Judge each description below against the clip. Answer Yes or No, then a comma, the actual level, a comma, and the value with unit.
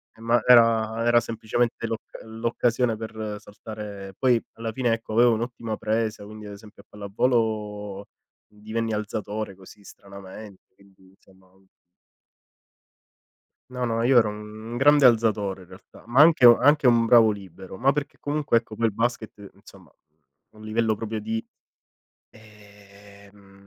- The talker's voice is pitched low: Yes, low, 110 Hz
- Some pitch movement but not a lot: No, narrow, 2.2 semitones